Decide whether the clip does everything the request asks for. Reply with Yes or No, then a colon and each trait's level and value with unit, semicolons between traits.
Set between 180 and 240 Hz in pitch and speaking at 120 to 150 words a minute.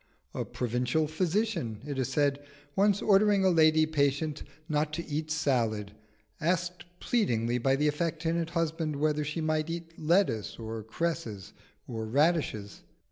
No: medium, 155 Hz; average, 140 wpm